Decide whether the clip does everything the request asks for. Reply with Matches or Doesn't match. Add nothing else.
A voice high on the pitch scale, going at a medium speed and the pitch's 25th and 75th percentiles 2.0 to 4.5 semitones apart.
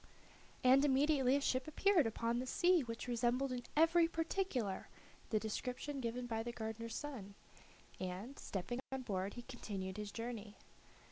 Matches